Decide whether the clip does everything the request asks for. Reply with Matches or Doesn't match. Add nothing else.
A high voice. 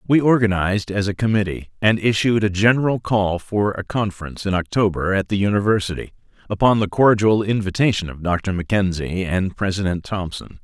Doesn't match